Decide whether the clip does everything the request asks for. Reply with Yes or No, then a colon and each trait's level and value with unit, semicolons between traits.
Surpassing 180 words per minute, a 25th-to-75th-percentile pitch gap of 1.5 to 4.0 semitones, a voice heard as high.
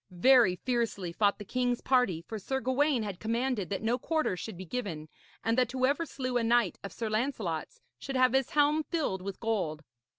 No: average, 195 wpm; average, 4.7 semitones; high, 235 Hz